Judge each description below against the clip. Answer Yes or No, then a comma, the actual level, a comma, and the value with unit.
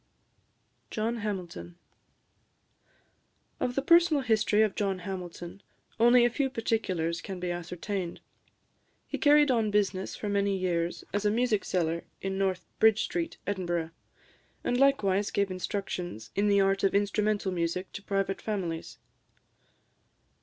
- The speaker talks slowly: Yes, slow, 130 wpm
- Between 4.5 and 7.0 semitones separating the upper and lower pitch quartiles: No, average, 3.3 semitones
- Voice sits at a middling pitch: No, high, 200 Hz